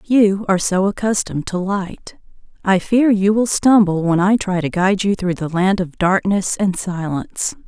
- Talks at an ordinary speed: Yes, average, 190 wpm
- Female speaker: Yes, female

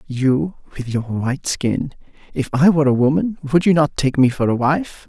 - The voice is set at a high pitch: No, medium, 140 Hz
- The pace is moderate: No, fast, 215 wpm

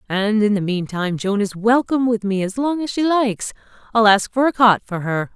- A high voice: Yes, high, 215 Hz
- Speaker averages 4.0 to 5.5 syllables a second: Yes, 5.3 syllables/s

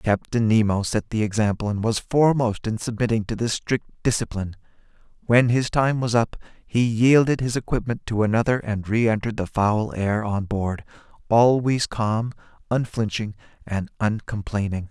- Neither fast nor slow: Yes, average, 150 wpm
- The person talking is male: Yes, male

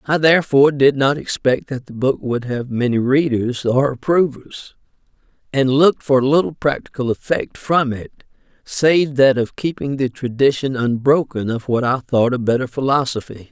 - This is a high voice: No, low, 130 Hz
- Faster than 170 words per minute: No, average, 160 wpm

